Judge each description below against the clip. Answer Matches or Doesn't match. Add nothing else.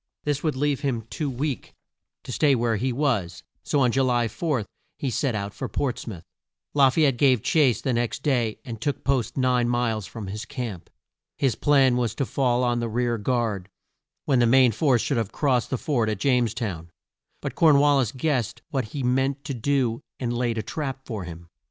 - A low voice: Matches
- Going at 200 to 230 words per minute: Matches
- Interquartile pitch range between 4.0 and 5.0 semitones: Doesn't match